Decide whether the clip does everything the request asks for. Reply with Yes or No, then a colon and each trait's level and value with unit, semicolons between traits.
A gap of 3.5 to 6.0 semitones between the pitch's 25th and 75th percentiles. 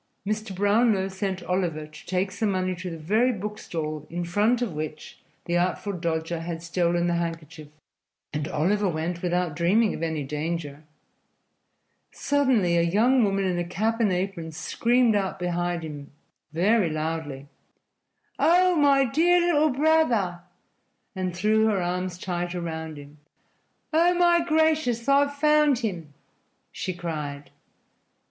Yes: wide, 5.4 semitones